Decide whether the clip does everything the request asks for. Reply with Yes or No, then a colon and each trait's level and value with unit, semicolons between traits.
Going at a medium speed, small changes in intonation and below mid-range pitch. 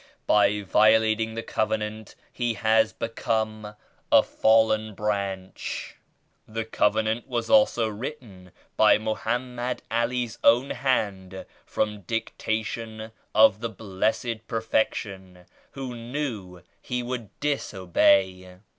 No: slow, 100 wpm; narrow, 2.0 semitones; low, 110 Hz